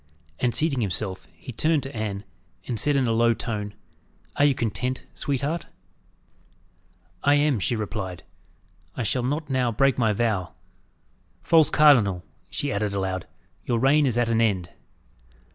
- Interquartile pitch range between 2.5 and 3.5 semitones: No, average, 4.8 semitones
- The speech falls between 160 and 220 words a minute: No, average, 150 wpm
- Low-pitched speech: Yes, low, 120 Hz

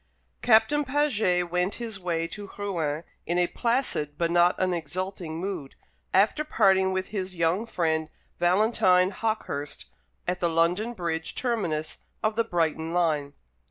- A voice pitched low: No, medium, 180 Hz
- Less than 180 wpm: Yes, average, 140 wpm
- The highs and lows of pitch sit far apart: No, average, 4.3 semitones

